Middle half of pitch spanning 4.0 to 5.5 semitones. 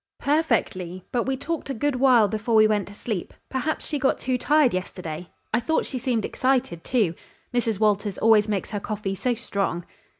Yes: average, 4.6 semitones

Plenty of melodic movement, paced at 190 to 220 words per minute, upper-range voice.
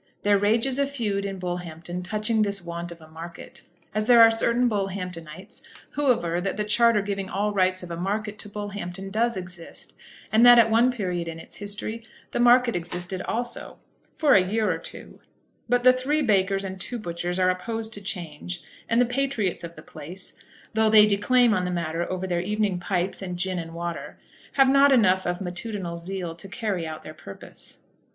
No: average, 4.2 semitones; average, 195 wpm; high, 195 Hz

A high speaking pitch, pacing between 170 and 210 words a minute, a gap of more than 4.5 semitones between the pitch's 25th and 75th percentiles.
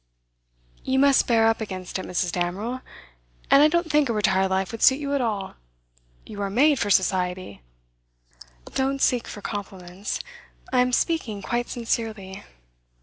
No: high, 220 Hz; average, 155 wpm; wide, 5.4 semitones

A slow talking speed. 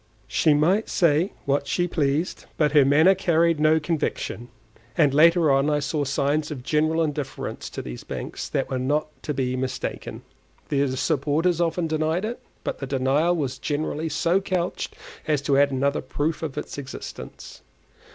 No: average, 165 wpm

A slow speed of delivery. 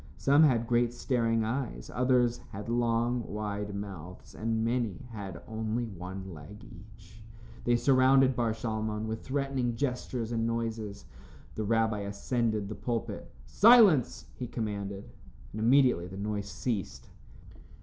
Yes: slow, 130 wpm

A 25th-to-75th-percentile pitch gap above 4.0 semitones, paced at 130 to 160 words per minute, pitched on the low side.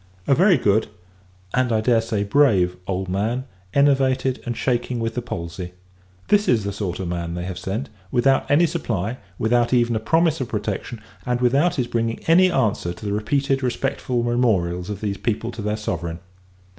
No: average, 4.6 semitones; average, 185 wpm; low, 115 Hz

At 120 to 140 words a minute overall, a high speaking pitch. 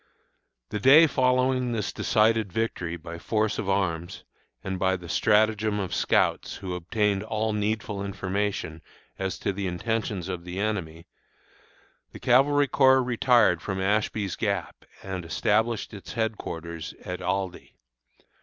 No: slow, 135 wpm; low, 100 Hz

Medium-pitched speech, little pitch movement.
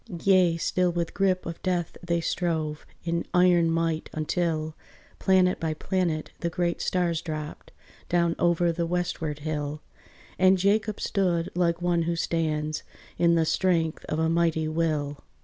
Yes: medium, 170 Hz; narrow, 2.0 semitones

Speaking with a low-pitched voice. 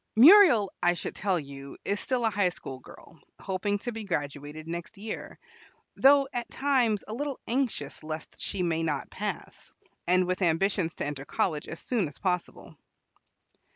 No: medium, 185 Hz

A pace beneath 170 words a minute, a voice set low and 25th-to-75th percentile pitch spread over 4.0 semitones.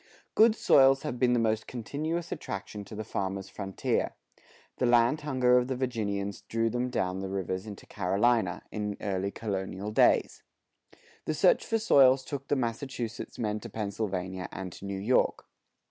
Yes: average, 160 wpm; low, 110 Hz; average, 4.6 semitones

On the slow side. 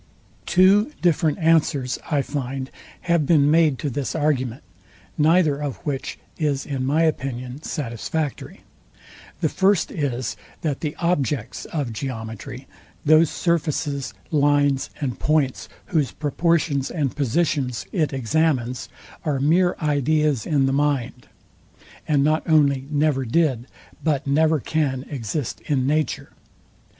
Yes: slow, 120 wpm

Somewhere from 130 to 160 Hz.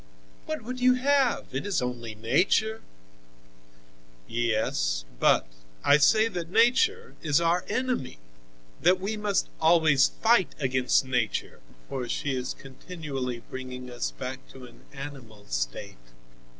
Yes: medium, 140 Hz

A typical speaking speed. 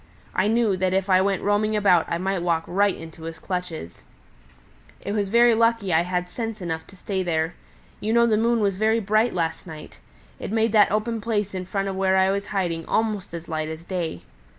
No: fast, 210 wpm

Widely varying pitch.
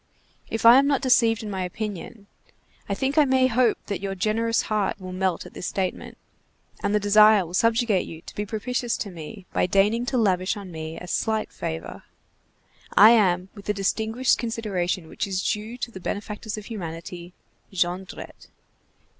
No: average, 3.6 semitones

